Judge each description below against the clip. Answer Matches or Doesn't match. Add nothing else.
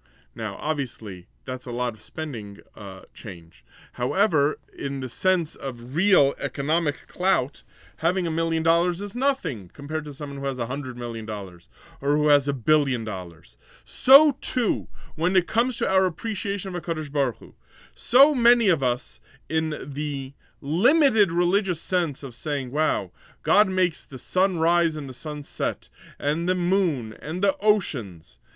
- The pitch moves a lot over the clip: Matches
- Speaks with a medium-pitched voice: Matches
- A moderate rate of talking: Matches